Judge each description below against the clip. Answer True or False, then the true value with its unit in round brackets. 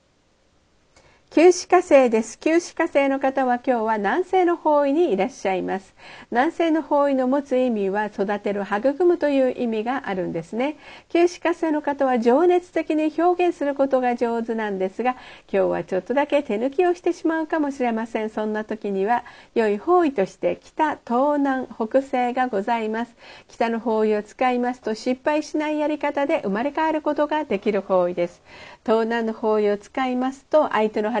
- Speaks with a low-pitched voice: False (255 Hz)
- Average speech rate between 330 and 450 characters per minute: True (350 characters per minute)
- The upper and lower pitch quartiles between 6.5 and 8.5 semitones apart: False (5.7 semitones)